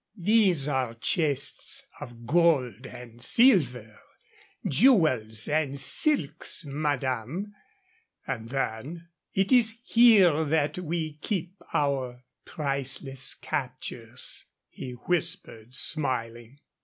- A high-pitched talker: No, medium, 145 Hz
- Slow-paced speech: Yes, slow, 90 wpm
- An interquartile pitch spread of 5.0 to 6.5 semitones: Yes, wide, 5.6 semitones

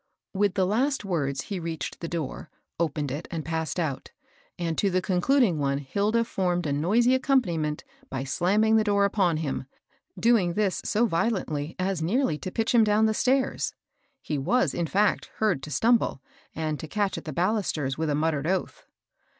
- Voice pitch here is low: No, medium, 180 Hz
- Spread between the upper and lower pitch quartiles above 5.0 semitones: Yes, wide, 5.5 semitones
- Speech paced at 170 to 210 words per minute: Yes, average, 180 wpm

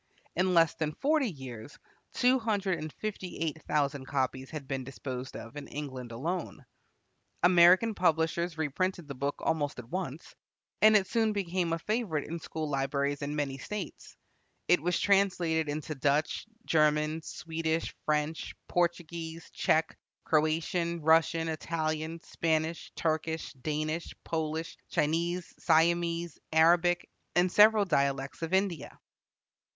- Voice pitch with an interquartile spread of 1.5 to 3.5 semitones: Yes, average, 2.9 semitones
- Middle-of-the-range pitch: Yes, medium, 160 Hz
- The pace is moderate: No, slow, 130 wpm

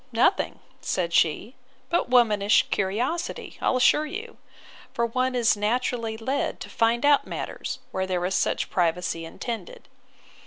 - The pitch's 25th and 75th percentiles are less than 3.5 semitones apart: No, average, 5.1 semitones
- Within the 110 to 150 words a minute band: Yes, average, 140 wpm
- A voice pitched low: No, high, 230 Hz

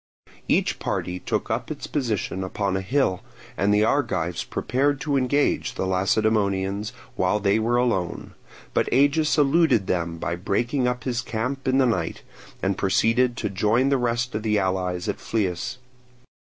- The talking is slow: No, average, 160 wpm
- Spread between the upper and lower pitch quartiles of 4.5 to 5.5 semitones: Yes, average, 5.0 semitones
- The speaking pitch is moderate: No, low, 110 Hz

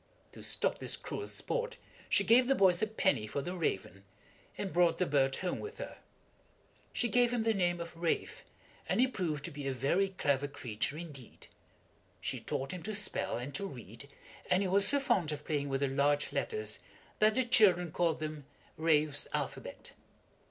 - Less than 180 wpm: No, average, 185 wpm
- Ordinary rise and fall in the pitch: No, wide, 6.3 semitones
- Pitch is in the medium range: Yes, medium, 170 Hz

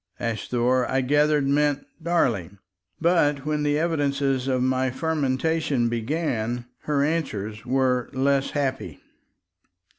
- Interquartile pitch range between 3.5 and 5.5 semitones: No, average, 2.9 semitones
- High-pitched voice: No, low, 135 Hz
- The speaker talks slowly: Yes, slow, 110 wpm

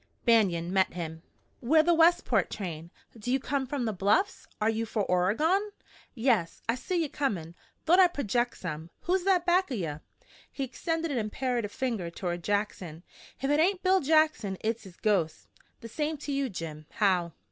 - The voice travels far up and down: Yes, wide, 8.8 semitones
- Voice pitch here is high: Yes, high, 230 Hz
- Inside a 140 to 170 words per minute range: No, average, 180 wpm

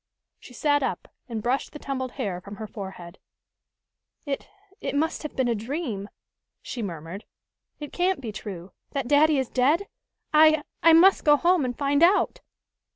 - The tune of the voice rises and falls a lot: Yes, wide, 6.0 semitones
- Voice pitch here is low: No, very high, 270 Hz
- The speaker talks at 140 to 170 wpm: Yes, average, 165 wpm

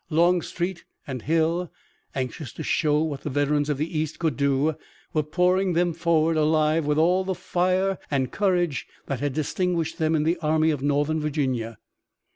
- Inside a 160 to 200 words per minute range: Yes, average, 170 wpm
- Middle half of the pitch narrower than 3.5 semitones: Yes, average, 2.8 semitones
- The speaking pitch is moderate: Yes, medium, 155 Hz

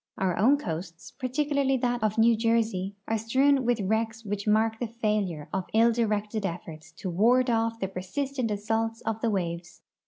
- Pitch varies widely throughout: No, average, 3.4 semitones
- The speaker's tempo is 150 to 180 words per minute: Yes, average, 175 wpm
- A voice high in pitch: Yes, high, 220 Hz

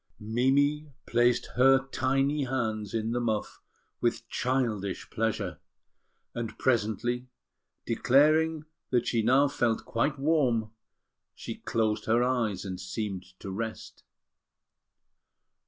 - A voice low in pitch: Yes, low, 120 Hz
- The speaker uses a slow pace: Yes, slow, 105 wpm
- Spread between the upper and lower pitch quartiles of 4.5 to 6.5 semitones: No, average, 3.4 semitones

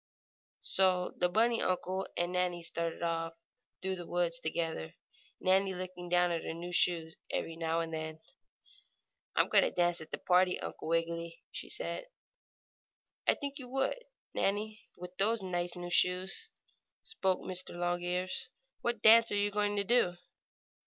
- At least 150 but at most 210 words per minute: Yes, average, 160 wpm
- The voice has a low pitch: No, medium, 180 Hz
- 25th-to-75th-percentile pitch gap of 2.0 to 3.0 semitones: Yes, narrow, 2.5 semitones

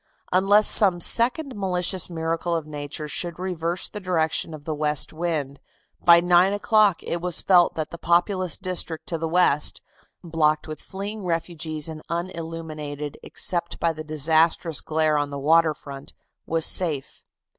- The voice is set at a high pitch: No, medium, 165 Hz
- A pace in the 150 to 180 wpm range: Yes, average, 155 wpm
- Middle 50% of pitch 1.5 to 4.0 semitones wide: Yes, narrow, 2.6 semitones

